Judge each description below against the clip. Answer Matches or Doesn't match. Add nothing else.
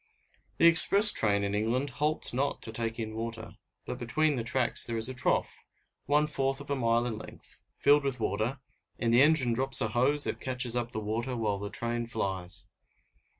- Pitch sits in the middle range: Doesn't match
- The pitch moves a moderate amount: Matches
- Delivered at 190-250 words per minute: Matches